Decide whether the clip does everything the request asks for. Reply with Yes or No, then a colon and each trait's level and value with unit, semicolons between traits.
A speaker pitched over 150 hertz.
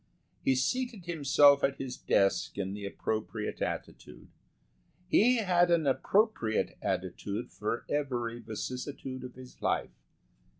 No: low, 130 Hz